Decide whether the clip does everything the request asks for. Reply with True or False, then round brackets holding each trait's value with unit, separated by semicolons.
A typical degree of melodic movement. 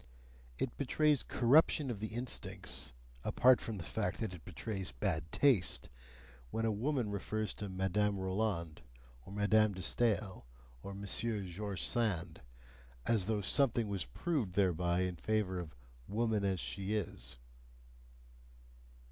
True (3.3 semitones)